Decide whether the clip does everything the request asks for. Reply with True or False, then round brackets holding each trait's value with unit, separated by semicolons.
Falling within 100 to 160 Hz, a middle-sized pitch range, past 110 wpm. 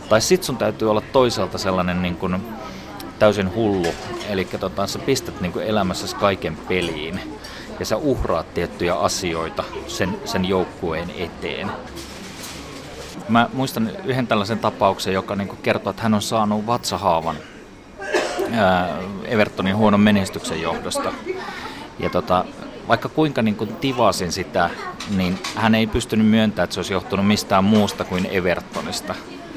True (105 Hz; 3.0 semitones; 140 wpm)